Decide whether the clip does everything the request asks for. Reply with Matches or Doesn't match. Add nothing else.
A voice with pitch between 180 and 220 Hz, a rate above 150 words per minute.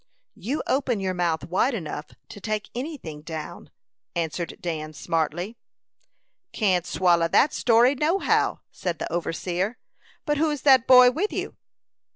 Doesn't match